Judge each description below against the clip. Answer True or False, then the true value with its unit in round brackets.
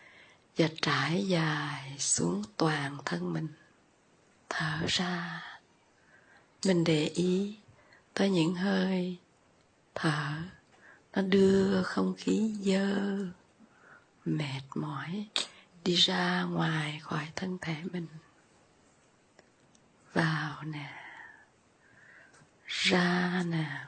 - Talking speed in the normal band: False (85 wpm)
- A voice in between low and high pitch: True (175 Hz)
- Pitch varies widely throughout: False (3.4 semitones)